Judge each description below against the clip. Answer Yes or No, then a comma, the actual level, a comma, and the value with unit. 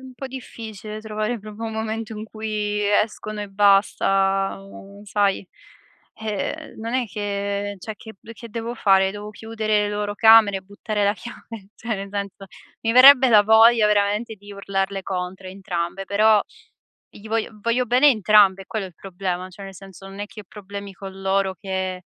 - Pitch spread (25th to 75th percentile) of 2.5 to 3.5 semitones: No, narrow, 2.1 semitones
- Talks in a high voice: Yes, high, 205 Hz